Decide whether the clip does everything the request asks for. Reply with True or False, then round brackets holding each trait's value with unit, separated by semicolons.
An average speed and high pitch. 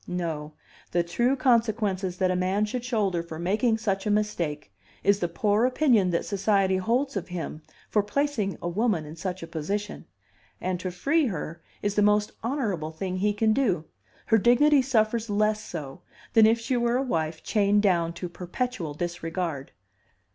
True (175 wpm; 200 Hz)